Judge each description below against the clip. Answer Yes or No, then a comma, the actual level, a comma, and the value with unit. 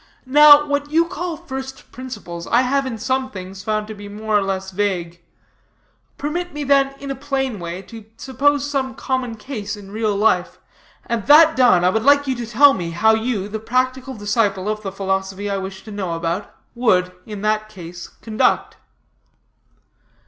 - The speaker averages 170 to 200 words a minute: Yes, average, 180 wpm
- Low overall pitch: No, high, 220 Hz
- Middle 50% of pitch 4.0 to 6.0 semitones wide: Yes, wide, 5.4 semitones